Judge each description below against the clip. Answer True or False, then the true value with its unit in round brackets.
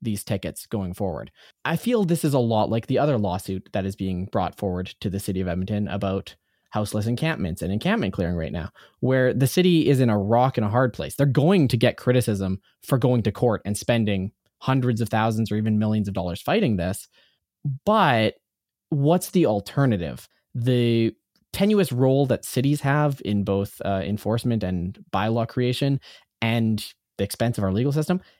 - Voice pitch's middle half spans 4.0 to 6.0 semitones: True (4.9 semitones)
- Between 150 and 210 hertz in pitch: False (115 Hz)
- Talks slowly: False (185 wpm)